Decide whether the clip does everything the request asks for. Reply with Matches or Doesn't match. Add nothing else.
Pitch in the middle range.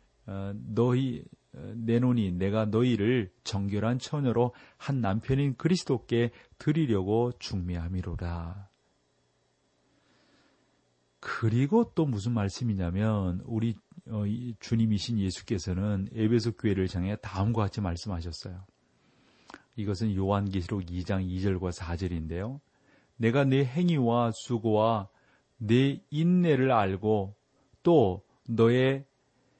Doesn't match